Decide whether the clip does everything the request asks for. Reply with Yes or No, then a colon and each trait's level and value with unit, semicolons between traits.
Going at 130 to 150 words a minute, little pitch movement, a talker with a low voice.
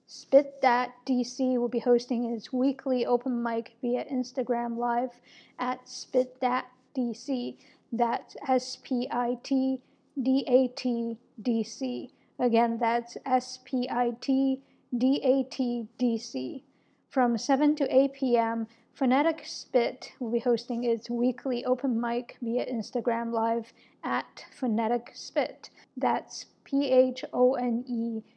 No: slow, 135 wpm; narrow, 1.7 semitones; very high, 250 Hz